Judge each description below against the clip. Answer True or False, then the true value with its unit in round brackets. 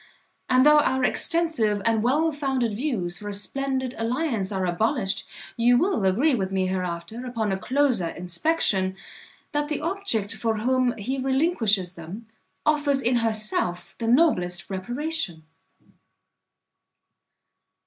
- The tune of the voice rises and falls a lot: True (6.2 semitones)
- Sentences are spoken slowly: True (130 wpm)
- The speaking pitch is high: True (235 Hz)